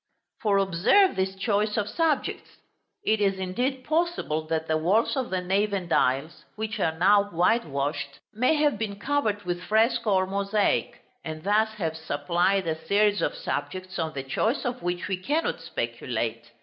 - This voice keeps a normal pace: Yes, average, 165 wpm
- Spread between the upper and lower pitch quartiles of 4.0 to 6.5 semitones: Yes, average, 4.3 semitones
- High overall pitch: Yes, high, 200 Hz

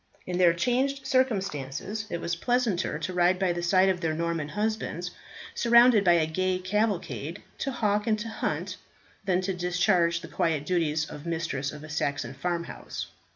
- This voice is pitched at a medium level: Yes, medium, 180 Hz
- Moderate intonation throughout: Yes, average, 3.9 semitones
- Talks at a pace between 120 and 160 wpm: No, average, 175 wpm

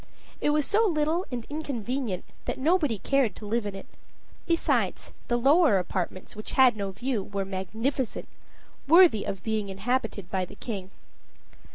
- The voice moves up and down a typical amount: No, wide, 6.3 semitones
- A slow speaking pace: No, average, 155 wpm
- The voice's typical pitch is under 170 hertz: No, high, 235 Hz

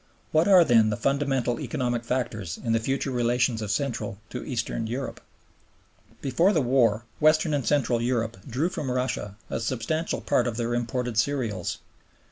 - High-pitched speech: No, low, 125 Hz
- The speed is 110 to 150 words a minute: No, average, 160 wpm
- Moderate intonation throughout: Yes, average, 3.2 semitones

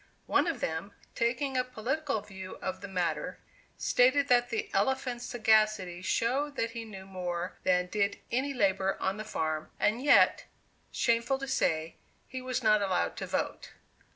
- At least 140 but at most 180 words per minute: Yes, average, 160 wpm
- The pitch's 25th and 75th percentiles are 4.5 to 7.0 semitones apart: Yes, average, 5.1 semitones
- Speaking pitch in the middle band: No, high, 220 Hz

